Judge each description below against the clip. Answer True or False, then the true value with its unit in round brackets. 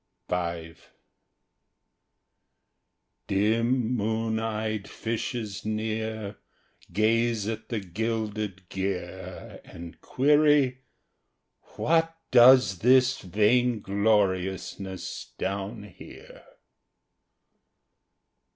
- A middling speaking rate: False (60 wpm)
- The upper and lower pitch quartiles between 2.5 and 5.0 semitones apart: True (3.2 semitones)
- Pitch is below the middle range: True (110 Hz)